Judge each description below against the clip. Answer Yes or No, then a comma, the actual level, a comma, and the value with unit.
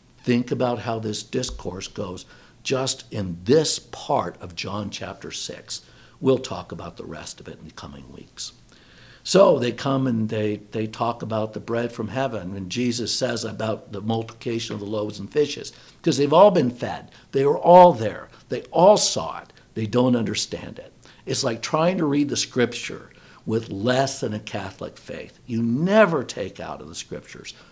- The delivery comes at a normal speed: Yes, average, 185 wpm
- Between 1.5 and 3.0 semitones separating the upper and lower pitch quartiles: No, average, 3.5 semitones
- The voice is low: Yes, low, 115 Hz